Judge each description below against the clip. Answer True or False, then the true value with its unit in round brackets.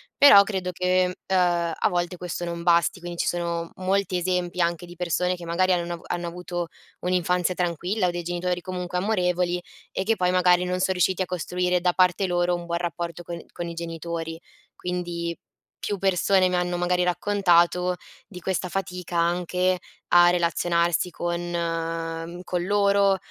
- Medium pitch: True (180 Hz)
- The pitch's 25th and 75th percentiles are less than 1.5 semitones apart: True (1.0 semitones)